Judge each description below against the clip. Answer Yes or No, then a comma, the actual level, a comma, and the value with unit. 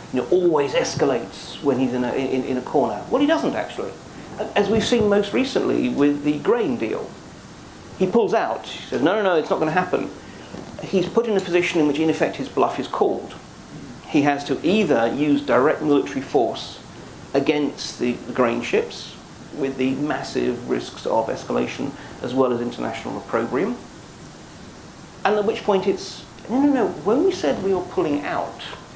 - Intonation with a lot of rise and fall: Yes, wide, 8.7 semitones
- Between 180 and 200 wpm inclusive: Yes, average, 185 wpm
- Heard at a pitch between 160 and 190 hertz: Yes, medium, 175 Hz